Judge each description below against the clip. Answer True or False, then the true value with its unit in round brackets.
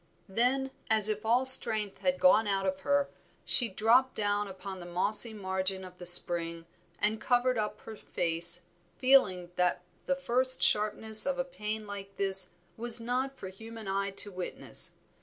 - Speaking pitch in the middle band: False (210 Hz)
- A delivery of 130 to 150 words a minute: False (165 wpm)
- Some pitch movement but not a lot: True (4.2 semitones)